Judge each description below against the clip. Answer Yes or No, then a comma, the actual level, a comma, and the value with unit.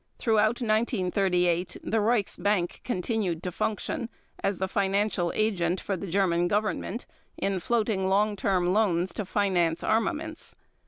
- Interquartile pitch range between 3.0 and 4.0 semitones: Yes, average, 3.3 semitones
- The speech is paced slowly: Yes, slow, 125 wpm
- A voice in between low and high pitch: No, high, 200 Hz